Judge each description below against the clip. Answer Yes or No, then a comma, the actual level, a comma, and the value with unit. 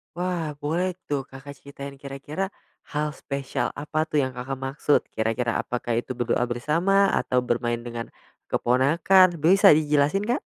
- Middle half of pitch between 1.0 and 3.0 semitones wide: No, average, 4.1 semitones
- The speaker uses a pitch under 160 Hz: Yes, medium, 140 Hz